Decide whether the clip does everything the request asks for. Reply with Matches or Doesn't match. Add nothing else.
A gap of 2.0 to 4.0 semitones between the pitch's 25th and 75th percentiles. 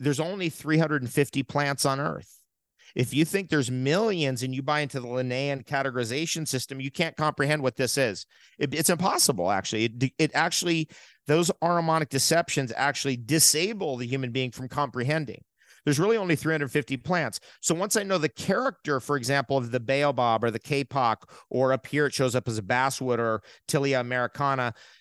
Matches